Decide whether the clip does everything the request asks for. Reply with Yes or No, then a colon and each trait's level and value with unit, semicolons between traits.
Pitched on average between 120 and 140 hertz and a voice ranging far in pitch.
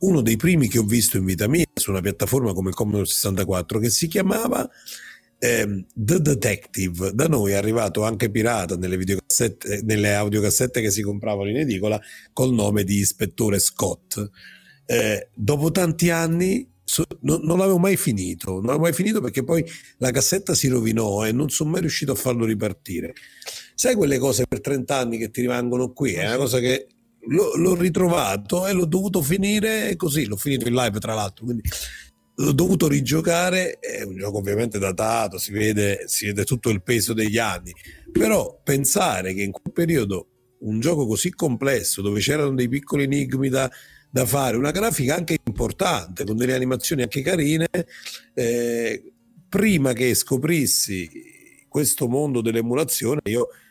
Yes: low, 125 Hz; wide, 7.2 semitones